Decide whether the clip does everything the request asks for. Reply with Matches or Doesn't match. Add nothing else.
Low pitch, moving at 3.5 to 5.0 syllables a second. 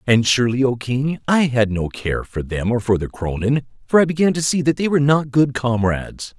Doesn't match